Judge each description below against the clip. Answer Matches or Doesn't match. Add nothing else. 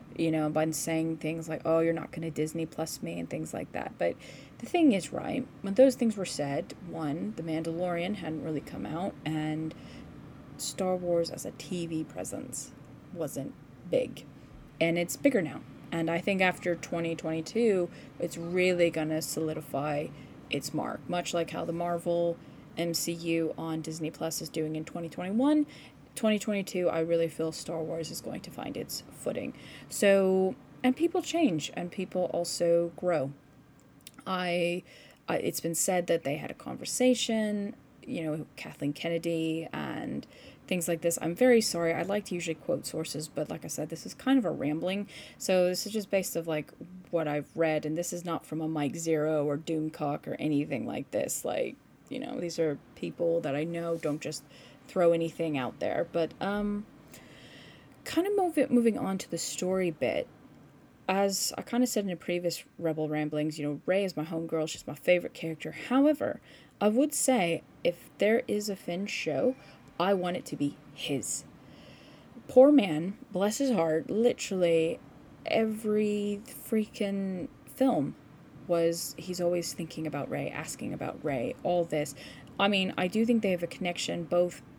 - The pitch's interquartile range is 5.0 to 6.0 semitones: Doesn't match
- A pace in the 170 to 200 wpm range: Matches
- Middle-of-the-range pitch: Matches